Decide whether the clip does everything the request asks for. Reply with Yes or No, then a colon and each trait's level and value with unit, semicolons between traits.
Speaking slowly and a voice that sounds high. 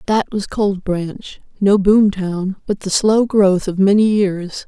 No: average, 165 wpm; high, 195 Hz